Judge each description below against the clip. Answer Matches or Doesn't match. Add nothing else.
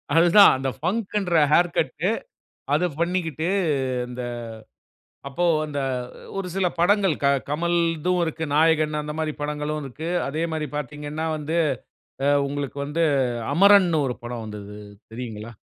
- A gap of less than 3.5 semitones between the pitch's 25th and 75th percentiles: Matches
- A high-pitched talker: Doesn't match